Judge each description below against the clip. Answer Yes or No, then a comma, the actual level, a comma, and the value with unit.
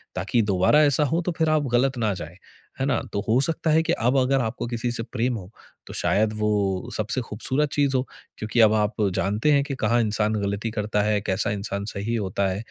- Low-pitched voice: Yes, low, 110 Hz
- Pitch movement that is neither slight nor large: Yes, average, 4.4 semitones